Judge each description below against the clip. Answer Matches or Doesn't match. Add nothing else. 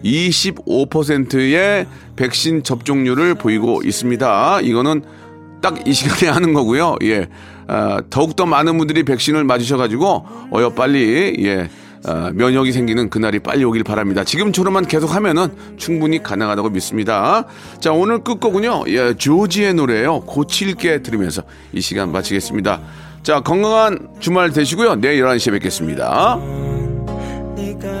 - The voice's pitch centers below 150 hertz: Matches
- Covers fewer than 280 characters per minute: Doesn't match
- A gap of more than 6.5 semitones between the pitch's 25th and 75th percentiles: Matches